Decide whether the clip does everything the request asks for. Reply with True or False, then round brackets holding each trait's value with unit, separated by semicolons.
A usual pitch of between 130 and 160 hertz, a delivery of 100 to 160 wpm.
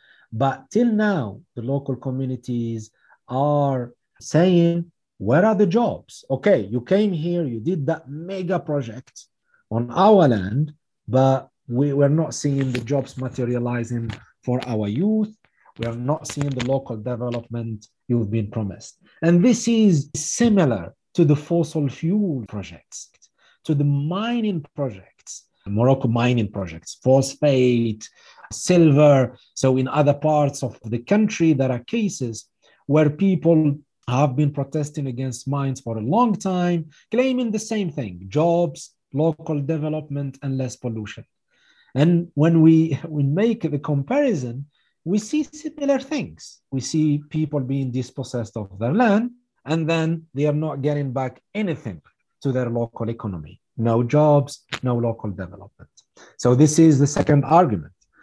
True (140 Hz; 140 wpm)